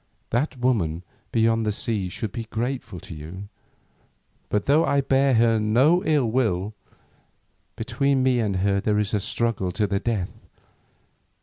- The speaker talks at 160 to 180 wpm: No, average, 150 wpm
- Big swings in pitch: No, average, 4.3 semitones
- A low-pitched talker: Yes, low, 115 Hz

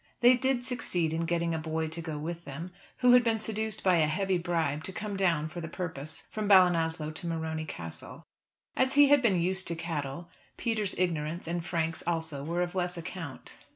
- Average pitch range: Yes, average, 3.1 semitones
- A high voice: No, medium, 170 Hz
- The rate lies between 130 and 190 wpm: No, average, 200 wpm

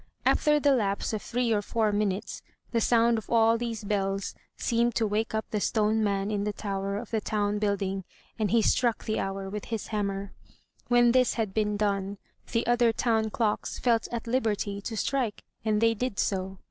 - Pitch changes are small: Yes, narrow, 2.3 semitones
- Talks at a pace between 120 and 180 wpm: No, average, 195 wpm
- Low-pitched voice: No, high, 215 Hz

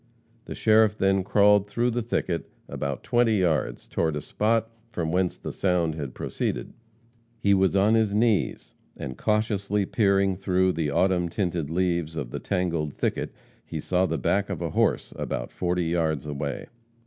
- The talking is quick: No, average, 165 wpm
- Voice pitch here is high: No, very low, 95 Hz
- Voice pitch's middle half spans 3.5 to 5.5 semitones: Yes, average, 3.9 semitones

